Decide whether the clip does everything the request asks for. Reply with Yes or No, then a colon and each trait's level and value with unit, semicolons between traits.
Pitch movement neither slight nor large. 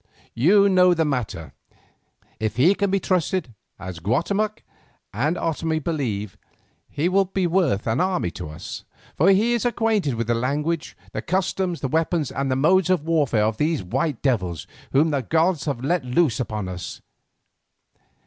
No: wide, 7.5 semitones